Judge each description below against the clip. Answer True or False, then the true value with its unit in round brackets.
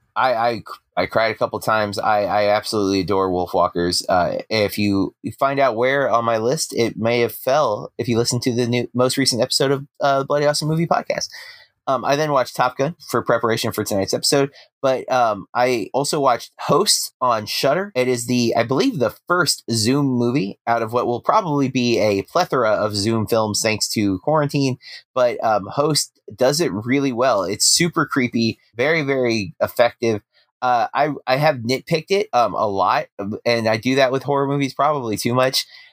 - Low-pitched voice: True (125 Hz)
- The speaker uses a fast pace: False (195 wpm)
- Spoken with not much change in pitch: False (3.9 semitones)